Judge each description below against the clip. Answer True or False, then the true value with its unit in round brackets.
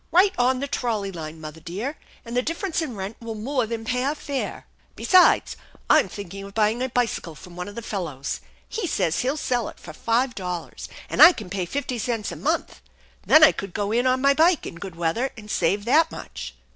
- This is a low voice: False (230 Hz)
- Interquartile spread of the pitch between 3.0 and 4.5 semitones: False (5.5 semitones)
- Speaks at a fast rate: True (220 wpm)